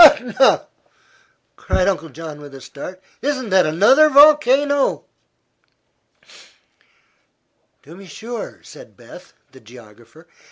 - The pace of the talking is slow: Yes, slow, 110 wpm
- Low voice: No, high, 190 Hz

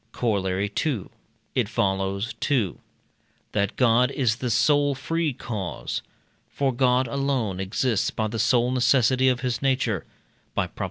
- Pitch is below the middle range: Yes, low, 120 Hz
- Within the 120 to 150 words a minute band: Yes, average, 140 wpm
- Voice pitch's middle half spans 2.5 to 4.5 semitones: Yes, average, 3.9 semitones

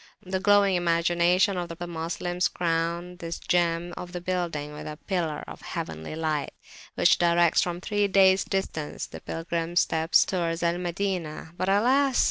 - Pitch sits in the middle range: Yes, medium, 175 Hz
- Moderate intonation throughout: No, narrow, 1.9 semitones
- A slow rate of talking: No, average, 155 wpm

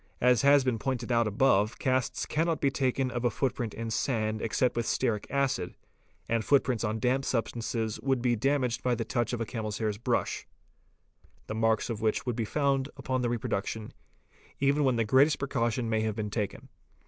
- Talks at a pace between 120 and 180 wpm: No, average, 195 wpm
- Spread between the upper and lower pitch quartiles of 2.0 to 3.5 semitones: Yes, average, 3.1 semitones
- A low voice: Yes, low, 120 Hz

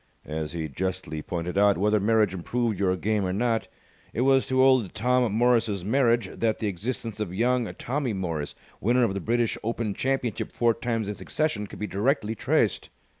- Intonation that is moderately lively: Yes, average, 4.0 semitones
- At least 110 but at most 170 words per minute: No, average, 180 wpm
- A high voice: No, low, 110 Hz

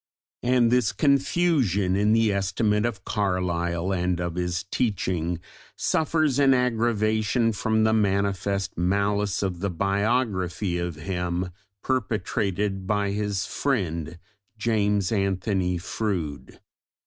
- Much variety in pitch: No, average, 3.4 semitones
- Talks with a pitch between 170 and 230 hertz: No, low, 100 Hz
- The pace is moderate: No, slow, 110 wpm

